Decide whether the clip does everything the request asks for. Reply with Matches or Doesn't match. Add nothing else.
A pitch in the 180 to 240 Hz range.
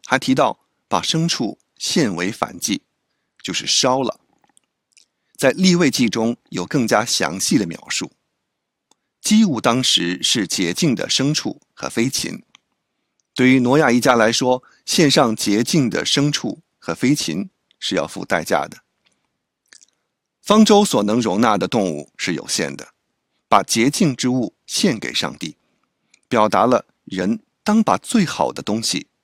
Doesn't match